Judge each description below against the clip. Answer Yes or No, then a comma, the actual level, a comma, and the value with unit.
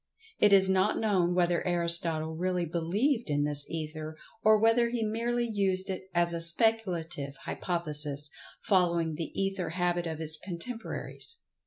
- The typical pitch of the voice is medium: Yes, medium, 175 Hz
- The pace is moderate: Yes, average, 145 wpm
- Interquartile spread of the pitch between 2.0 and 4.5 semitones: Yes, average, 4.0 semitones